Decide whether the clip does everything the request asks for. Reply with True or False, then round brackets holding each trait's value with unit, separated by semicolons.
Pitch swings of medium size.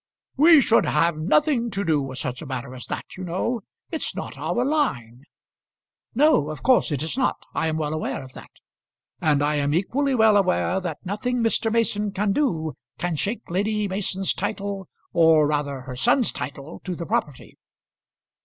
False (7.1 semitones)